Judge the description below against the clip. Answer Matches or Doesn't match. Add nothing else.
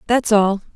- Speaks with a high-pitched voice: Matches